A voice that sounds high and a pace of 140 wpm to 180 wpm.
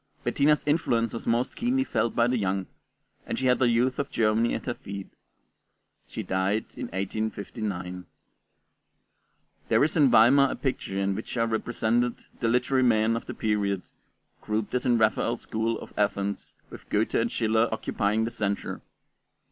No: low, 115 Hz; average, 165 wpm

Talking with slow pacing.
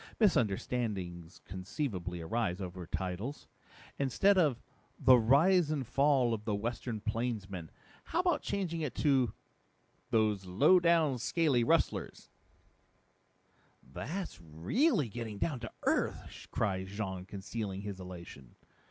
Yes: slow, 110 wpm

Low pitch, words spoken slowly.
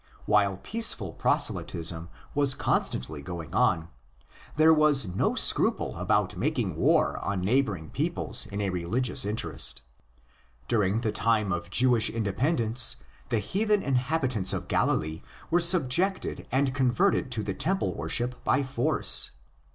Yes: low, 115 Hz; slow, 130 wpm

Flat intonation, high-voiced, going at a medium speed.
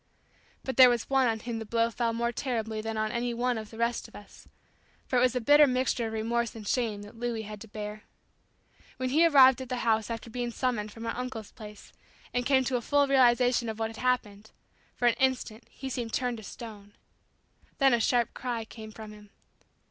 No: narrow, 2.3 semitones; high, 235 Hz; fast, 220 wpm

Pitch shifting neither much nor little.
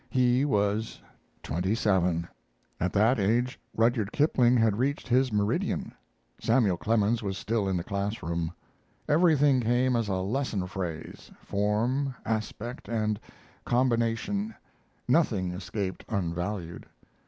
Yes: average, 4.3 semitones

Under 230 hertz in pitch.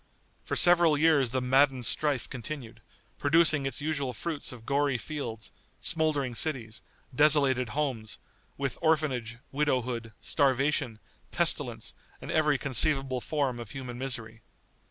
Yes: low, 135 Hz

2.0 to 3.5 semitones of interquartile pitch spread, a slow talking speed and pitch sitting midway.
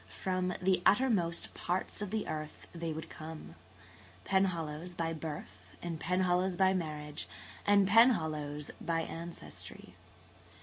Yes: average, 3.2 semitones; slow, 115 wpm; medium, 170 Hz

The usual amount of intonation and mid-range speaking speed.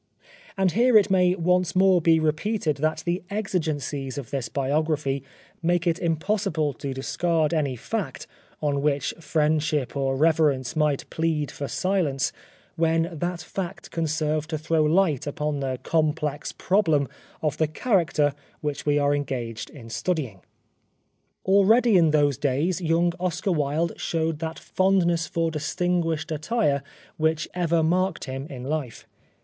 Yes: average, 3.2 semitones; average, 145 wpm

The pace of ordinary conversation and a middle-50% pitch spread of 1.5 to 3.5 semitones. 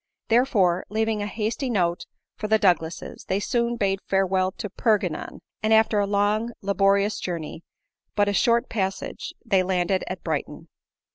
Yes: average, 150 wpm; average, 2.9 semitones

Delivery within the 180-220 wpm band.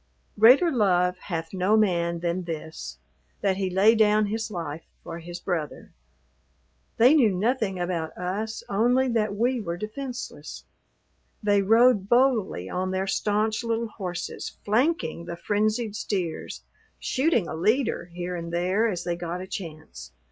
No: average, 145 wpm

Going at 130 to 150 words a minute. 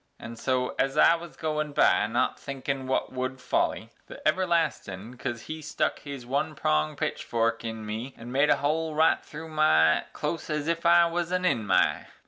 No: average, 180 wpm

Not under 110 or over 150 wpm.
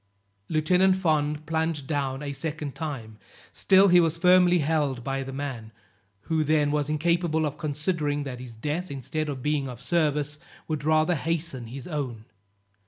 No: average, 160 wpm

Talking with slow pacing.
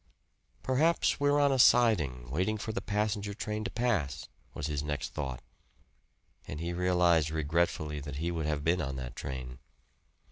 No: average, 165 wpm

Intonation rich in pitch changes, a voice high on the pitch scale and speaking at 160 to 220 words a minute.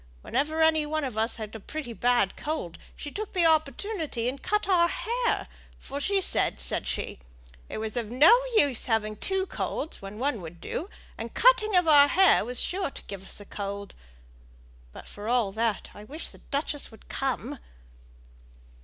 Yes: wide, 6.7 semitones; very high, 275 Hz; average, 180 wpm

